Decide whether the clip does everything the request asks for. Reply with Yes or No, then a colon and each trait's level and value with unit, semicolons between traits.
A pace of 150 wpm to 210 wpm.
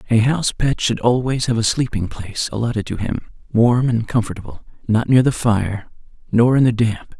Yes: average, 190 wpm